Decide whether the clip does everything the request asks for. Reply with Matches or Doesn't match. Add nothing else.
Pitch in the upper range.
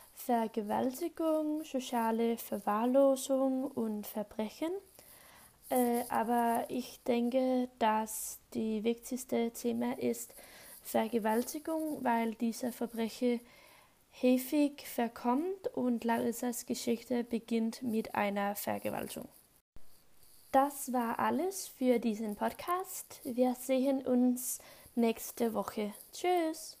Matches